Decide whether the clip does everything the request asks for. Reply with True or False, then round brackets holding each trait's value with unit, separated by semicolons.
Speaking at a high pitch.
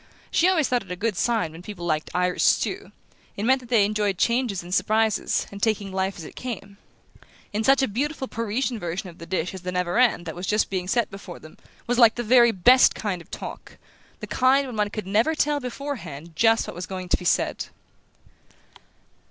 True (210 Hz)